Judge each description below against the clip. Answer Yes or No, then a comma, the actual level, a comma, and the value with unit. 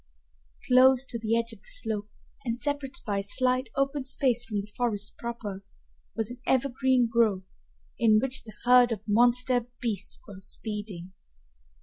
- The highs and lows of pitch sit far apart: No, average, 3.3 semitones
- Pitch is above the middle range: Yes, high, 235 Hz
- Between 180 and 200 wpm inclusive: No, average, 155 wpm